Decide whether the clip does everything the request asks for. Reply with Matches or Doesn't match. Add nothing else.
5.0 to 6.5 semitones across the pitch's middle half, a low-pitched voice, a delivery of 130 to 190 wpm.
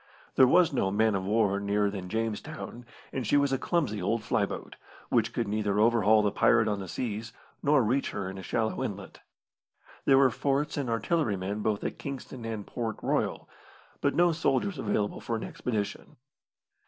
Doesn't match